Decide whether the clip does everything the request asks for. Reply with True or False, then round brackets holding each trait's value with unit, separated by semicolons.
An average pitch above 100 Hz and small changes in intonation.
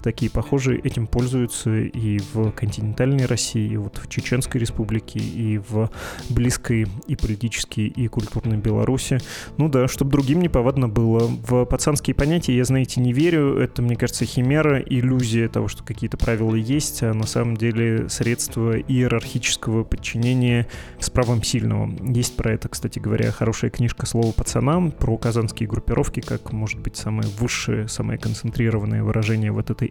True (115 Hz; 2.2 semitones)